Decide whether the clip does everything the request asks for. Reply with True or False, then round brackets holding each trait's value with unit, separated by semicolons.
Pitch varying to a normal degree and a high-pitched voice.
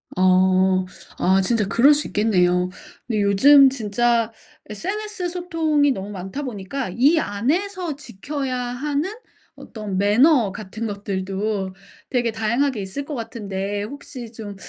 False (6.1 semitones; 225 Hz)